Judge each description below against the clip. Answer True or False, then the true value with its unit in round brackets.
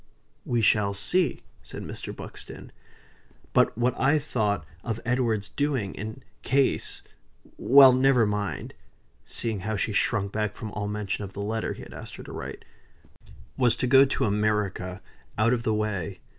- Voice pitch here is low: True (110 Hz)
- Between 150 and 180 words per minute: True (160 wpm)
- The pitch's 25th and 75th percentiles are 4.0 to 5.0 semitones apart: False (3.3 semitones)